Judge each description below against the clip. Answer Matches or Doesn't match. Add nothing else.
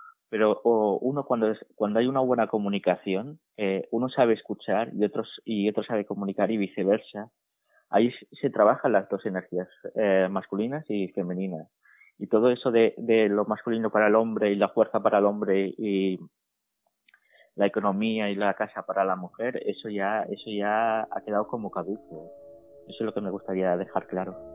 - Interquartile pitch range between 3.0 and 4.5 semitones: Doesn't match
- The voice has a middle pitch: Doesn't match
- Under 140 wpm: Doesn't match